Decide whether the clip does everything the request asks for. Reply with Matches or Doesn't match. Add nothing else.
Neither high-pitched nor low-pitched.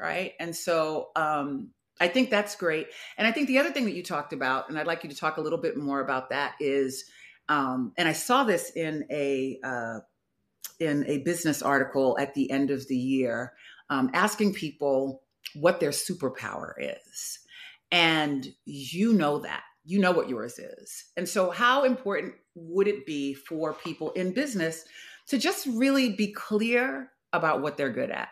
Matches